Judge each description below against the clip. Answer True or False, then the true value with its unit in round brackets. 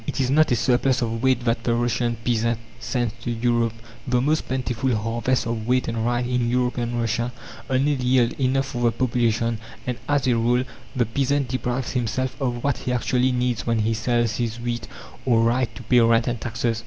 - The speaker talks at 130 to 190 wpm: False (200 wpm)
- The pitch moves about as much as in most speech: False (1.5 semitones)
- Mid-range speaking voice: False (120 Hz)